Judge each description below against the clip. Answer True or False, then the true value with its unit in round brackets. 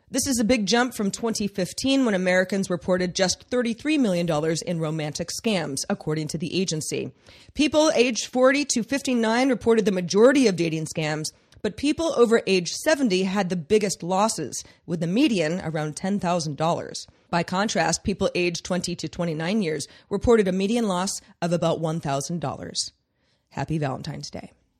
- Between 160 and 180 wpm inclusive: False (150 wpm)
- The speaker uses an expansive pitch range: True (5.8 semitones)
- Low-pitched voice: False (185 Hz)